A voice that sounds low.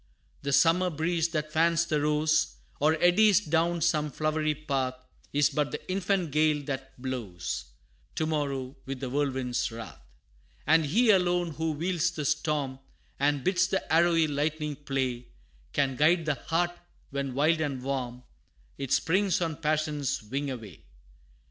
No: medium, 150 Hz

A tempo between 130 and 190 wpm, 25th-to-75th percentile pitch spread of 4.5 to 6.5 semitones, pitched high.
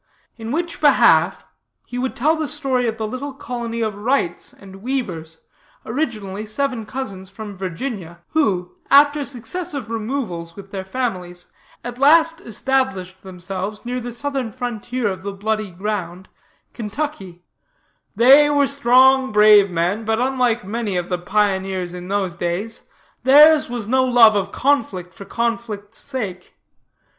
Yes: average, 140 wpm; wide, 5.4 semitones; high, 225 Hz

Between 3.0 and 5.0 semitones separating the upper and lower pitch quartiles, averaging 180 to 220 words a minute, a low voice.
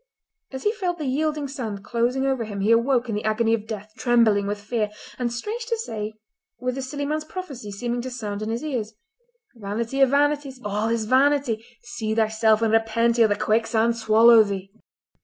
No: average, 3.6 semitones; average, 195 wpm; high, 230 Hz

